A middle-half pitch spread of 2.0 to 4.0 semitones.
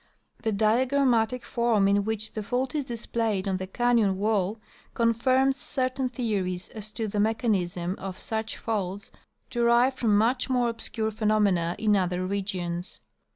Yes: average, 3.3 semitones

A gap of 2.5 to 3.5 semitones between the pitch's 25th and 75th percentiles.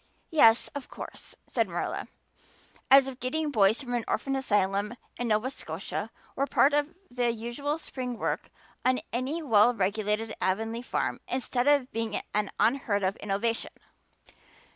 No: average, 4.1 semitones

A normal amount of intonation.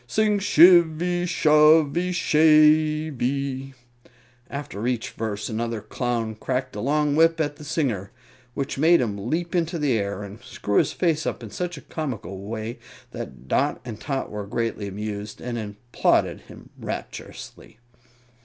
No: wide, 6.3 semitones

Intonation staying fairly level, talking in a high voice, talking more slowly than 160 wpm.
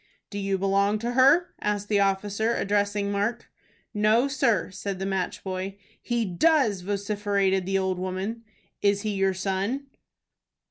Yes: narrow, 2.2 semitones; high, 200 Hz; average, 145 wpm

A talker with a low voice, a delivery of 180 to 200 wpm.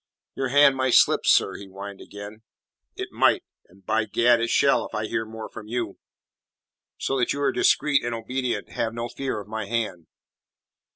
Yes: low, 115 Hz; average, 185 wpm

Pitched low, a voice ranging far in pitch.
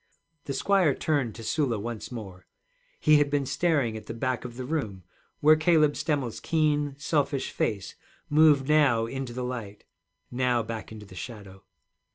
No: low, 130 Hz; average, 4.7 semitones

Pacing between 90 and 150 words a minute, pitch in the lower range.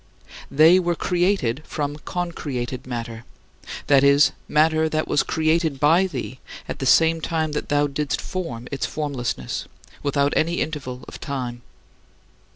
No: average, 140 wpm; medium, 150 Hz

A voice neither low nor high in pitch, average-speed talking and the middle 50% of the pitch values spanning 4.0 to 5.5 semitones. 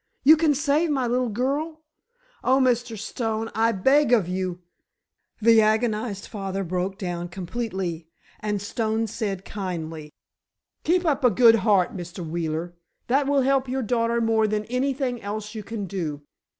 No: high, 220 Hz; average, 150 wpm; average, 4.9 semitones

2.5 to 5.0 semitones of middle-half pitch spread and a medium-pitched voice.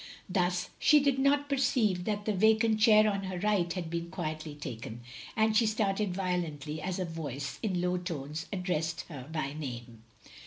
No: wide, 5.4 semitones; medium, 180 Hz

